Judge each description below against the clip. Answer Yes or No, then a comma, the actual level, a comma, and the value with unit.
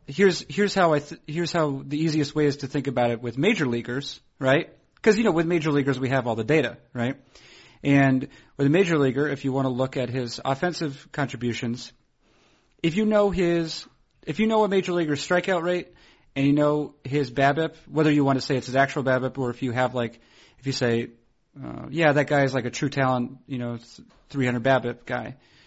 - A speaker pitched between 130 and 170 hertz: Yes, medium, 140 Hz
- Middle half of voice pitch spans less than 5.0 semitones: Yes, average, 3.7 semitones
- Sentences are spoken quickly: Yes, fast, 215 wpm